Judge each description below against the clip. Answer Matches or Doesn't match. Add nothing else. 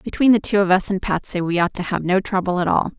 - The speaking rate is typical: Doesn't match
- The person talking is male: Doesn't match